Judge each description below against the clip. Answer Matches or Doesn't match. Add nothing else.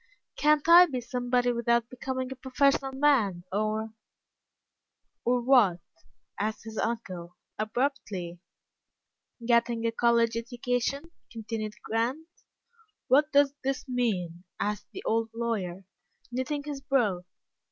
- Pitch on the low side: Doesn't match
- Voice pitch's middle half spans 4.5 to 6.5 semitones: Doesn't match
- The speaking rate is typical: Doesn't match